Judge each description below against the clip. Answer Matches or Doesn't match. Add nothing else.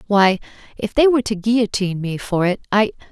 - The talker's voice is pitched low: Doesn't match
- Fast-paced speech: Doesn't match